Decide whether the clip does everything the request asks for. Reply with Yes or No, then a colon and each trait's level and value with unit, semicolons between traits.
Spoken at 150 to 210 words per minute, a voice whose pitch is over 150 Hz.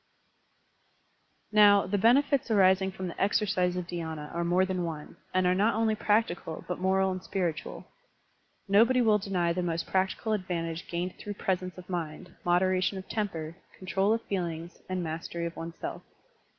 Yes: average, 160 wpm; medium, 185 Hz